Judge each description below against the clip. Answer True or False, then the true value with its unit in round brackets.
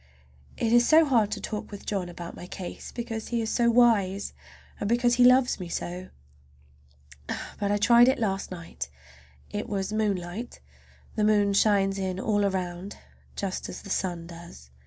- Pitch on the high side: True (205 Hz)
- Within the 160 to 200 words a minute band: True (170 wpm)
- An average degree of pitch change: True (3.8 semitones)